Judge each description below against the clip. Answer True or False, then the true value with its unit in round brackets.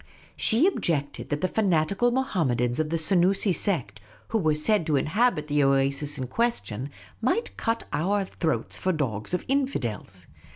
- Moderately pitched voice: True (160 Hz)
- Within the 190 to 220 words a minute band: False (155 wpm)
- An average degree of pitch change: False (7.2 semitones)